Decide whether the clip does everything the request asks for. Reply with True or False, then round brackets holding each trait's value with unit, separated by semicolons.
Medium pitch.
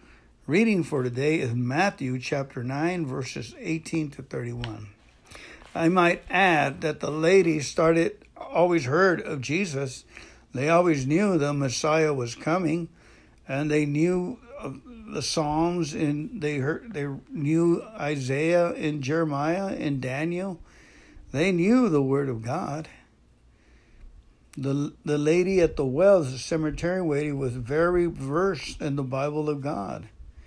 True (155 Hz)